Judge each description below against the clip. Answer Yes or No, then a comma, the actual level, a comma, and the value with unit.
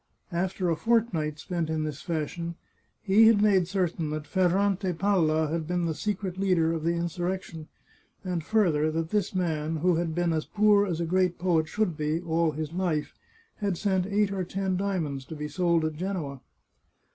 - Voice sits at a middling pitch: Yes, medium, 175 Hz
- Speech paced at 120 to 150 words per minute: No, average, 180 wpm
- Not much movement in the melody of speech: No, average, 3.2 semitones